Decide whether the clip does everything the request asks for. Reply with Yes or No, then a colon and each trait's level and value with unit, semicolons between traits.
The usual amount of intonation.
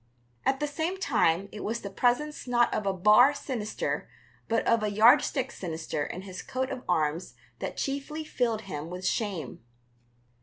No: wide, 6.2 semitones